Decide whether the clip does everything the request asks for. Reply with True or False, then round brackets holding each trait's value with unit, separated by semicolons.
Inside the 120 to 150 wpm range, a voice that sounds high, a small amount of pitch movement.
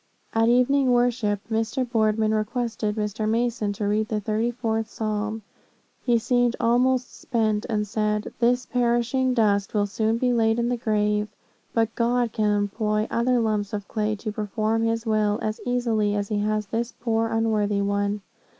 False (170 wpm; 220 Hz; 2.1 semitones)